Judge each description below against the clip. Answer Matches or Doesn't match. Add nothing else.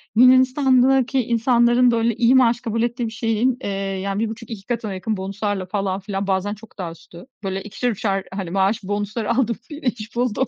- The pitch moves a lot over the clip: Doesn't match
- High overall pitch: Matches